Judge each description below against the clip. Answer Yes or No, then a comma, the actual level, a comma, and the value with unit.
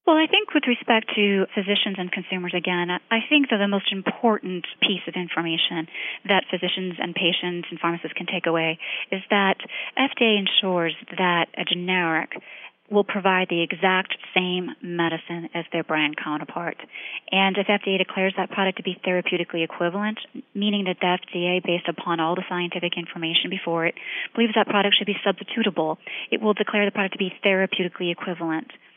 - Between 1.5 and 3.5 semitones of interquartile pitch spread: Yes, average, 3.0 semitones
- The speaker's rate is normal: Yes, average, 170 wpm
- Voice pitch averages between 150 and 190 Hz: Yes, medium, 185 Hz